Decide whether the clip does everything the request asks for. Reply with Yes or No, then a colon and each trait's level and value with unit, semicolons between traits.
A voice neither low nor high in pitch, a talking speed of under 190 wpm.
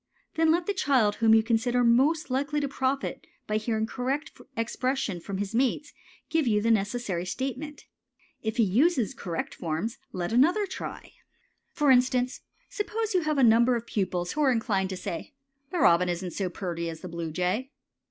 No: high, 235 Hz; average, 175 wpm